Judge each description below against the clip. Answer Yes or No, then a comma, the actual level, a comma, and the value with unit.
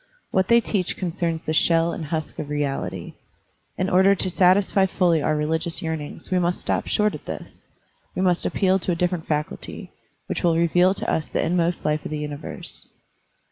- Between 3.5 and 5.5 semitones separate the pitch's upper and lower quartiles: No, average, 2.9 semitones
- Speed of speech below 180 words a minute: No, average, 190 wpm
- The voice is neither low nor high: Yes, medium, 170 Hz